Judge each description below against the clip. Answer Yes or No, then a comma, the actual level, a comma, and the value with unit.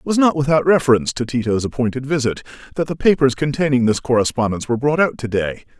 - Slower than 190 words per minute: No, fast, 205 wpm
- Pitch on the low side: Yes, low, 130 Hz